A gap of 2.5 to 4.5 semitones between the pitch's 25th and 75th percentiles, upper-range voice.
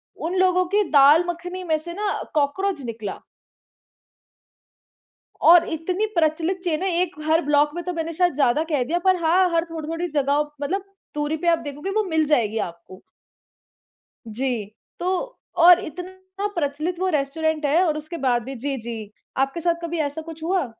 Yes: average, 3.8 semitones; very high, 320 Hz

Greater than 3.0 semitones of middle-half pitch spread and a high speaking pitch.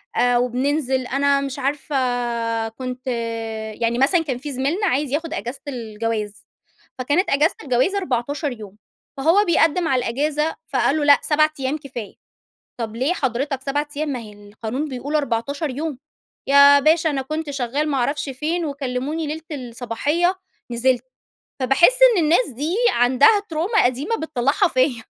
Yes: average, 3.7 semitones; very high, 280 Hz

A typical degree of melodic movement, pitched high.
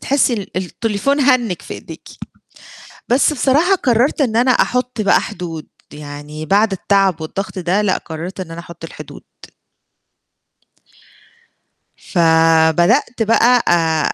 No: wide, 6.5 semitones; high, 200 Hz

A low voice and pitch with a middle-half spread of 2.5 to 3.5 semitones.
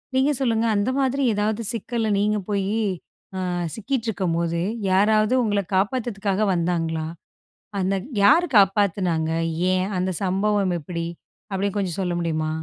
No: high, 200 Hz; average, 3.2 semitones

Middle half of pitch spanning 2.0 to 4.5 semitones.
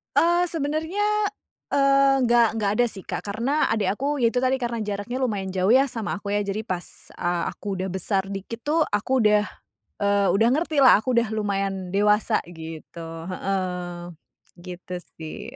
No: average, 5.0 semitones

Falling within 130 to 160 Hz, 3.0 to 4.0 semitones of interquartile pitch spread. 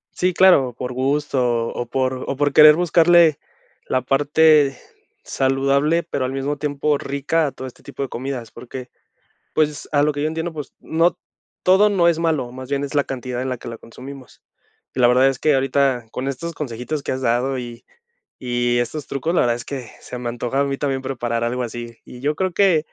Yes: low, 135 Hz; average, 3.3 semitones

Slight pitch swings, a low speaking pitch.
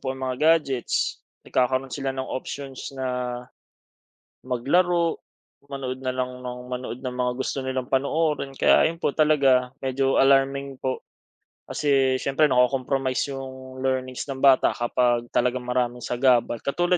Yes: narrow, 1.3 semitones; low, 130 Hz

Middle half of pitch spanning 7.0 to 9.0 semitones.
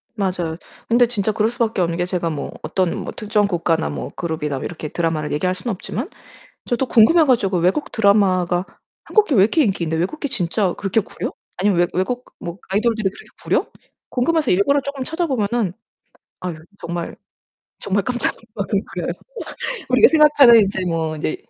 No: wide, 5.6 semitones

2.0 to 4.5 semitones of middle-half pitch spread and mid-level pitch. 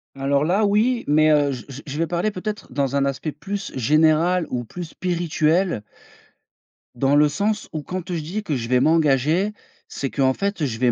No: average, 4.9 semitones; medium, 155 Hz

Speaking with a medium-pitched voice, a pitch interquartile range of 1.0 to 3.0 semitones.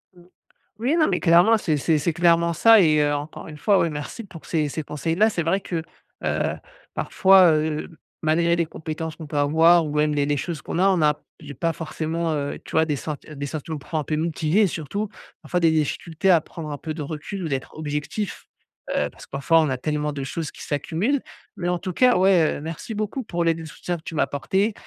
Yes: medium, 160 Hz; average, 2.7 semitones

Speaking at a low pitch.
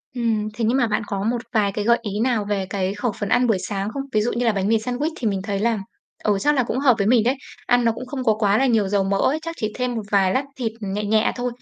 No: high, 220 Hz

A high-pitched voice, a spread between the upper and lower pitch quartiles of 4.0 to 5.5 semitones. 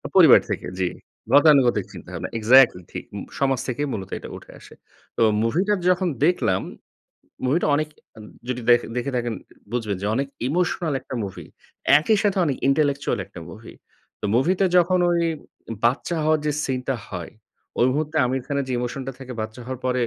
No: low, 135 Hz; average, 4.3 semitones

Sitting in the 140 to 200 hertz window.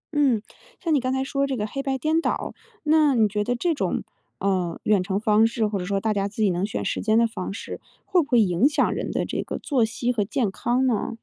No: high, 225 Hz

